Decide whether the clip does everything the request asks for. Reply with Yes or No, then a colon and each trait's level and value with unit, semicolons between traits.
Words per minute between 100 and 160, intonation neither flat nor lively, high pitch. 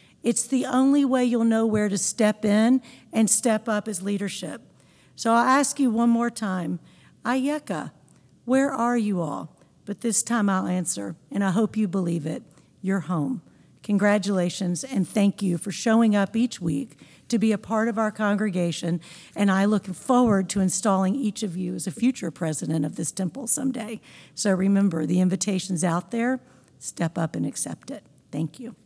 No: average, 180 wpm; average, 4.2 semitones; high, 205 Hz